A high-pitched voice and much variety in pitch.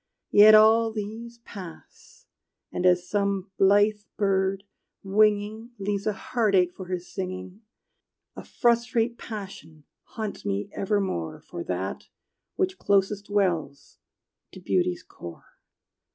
No: high, 200 Hz; average, 2.8 semitones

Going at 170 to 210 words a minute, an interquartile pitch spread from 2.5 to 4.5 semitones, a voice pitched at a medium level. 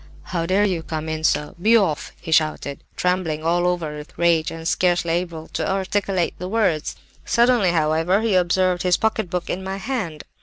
Yes: average, 180 wpm; average, 3.0 semitones; medium, 175 Hz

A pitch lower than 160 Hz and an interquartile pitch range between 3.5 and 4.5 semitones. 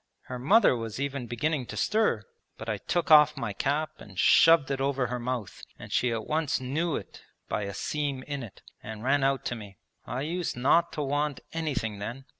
Yes: low, 135 Hz; average, 4.2 semitones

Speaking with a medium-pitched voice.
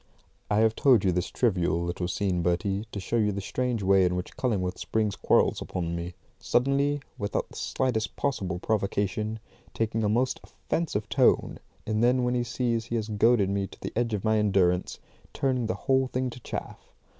No: low, 110 Hz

